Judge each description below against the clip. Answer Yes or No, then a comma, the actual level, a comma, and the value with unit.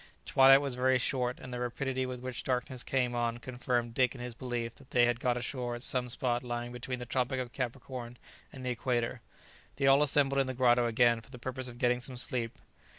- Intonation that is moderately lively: No, narrow, 1.3 semitones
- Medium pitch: No, low, 125 Hz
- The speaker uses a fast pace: Yes, fast, 220 wpm